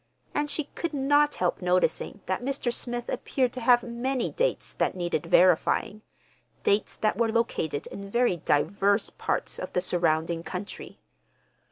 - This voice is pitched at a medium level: No, high, 215 Hz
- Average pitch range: No, wide, 5.7 semitones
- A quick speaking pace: No, average, 145 wpm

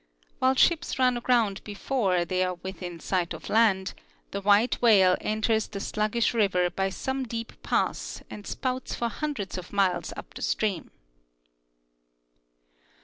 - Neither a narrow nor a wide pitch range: Yes, average, 3.9 semitones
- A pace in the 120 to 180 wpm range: Yes, average, 145 wpm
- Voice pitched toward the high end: Yes, high, 210 Hz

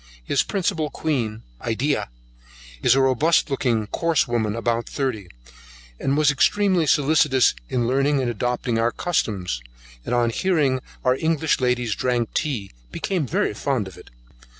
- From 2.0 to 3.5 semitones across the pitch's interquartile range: No, average, 4.3 semitones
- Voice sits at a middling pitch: No, low, 130 Hz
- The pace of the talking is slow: No, average, 145 wpm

